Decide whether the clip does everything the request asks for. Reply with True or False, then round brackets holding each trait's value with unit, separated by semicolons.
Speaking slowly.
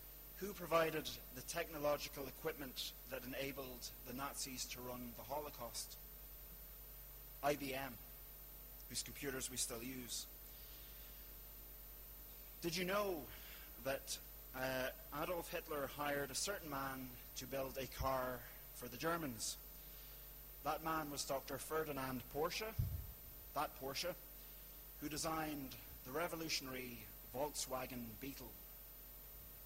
True (105 wpm)